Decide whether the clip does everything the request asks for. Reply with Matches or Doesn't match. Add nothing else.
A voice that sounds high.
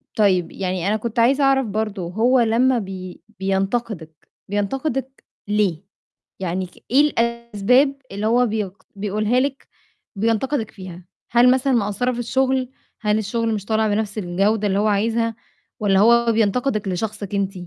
Matches